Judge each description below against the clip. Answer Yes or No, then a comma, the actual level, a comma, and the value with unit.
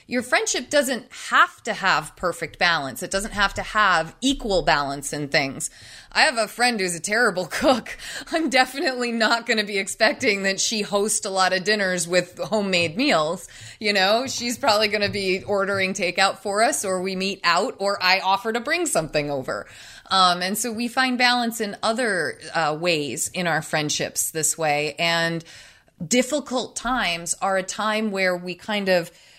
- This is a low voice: No, high, 200 Hz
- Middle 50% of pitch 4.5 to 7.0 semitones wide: Yes, average, 4.9 semitones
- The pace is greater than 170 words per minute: Yes, average, 180 wpm